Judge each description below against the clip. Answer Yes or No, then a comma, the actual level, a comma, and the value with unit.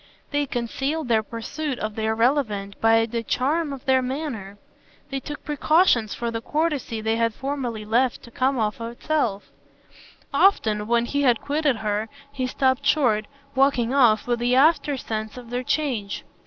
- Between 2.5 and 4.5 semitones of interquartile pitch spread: Yes, average, 4.1 semitones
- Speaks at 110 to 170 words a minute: Yes, average, 160 wpm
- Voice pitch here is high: Yes, high, 245 Hz